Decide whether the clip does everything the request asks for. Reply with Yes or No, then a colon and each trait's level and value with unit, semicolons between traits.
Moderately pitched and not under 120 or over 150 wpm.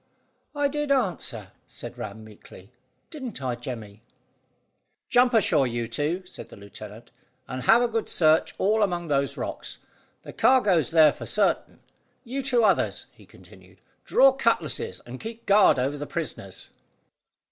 Yes: medium, 165 Hz; average, 145 wpm